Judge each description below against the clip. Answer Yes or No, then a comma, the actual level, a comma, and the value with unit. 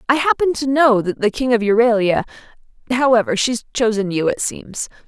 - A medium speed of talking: Yes, average, 165 wpm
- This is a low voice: No, high, 230 Hz